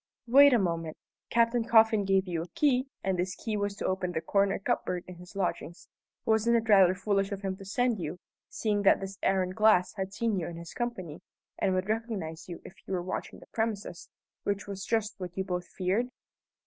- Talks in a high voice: Yes, high, 195 Hz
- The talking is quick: Yes, fast, 210 wpm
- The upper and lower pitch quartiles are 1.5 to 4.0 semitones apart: Yes, average, 3.3 semitones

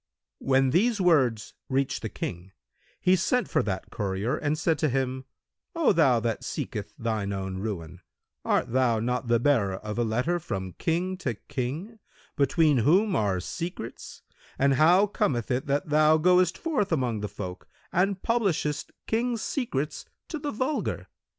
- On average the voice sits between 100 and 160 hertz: Yes, medium, 140 Hz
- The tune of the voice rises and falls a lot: Yes, wide, 8.2 semitones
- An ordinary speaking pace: Yes, average, 155 wpm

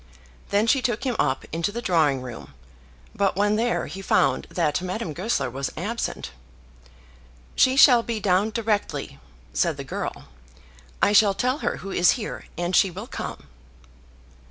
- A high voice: Yes, high, 205 Hz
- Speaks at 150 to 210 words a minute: Yes, average, 155 wpm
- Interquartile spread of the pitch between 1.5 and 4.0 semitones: No, average, 4.8 semitones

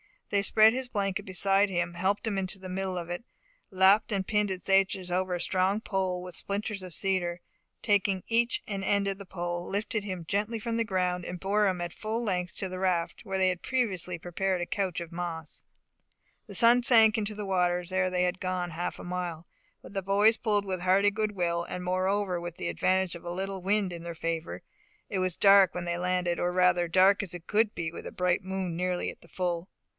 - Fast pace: Yes, fast, 225 wpm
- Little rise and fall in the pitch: Yes, narrow, 2.2 semitones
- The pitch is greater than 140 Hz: Yes, medium, 185 Hz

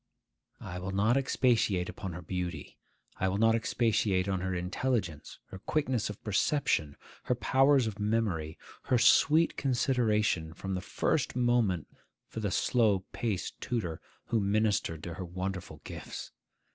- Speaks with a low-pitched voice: Yes, low, 105 Hz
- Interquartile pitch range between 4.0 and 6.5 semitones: Yes, average, 4.6 semitones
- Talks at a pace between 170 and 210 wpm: No, average, 145 wpm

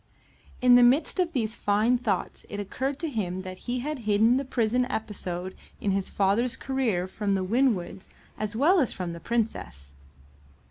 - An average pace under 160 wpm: No, average, 175 wpm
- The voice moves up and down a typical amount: Yes, average, 4.7 semitones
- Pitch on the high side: Yes, high, 220 Hz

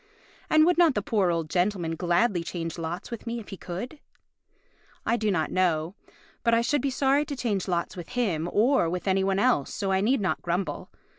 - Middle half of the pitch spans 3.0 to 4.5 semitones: No, wide, 5.6 semitones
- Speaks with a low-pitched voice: No, high, 195 Hz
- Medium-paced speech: No, fast, 210 wpm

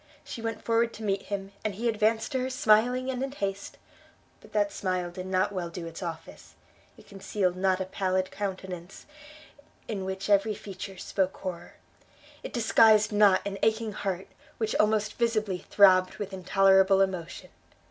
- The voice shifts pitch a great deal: No, narrow, 2.5 semitones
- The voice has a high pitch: Yes, high, 195 Hz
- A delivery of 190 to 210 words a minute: No, average, 165 wpm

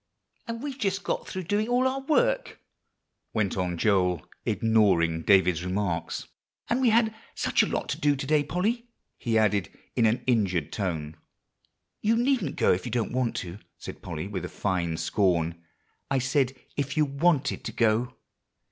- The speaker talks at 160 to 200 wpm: Yes, average, 170 wpm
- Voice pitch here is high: No, low, 115 Hz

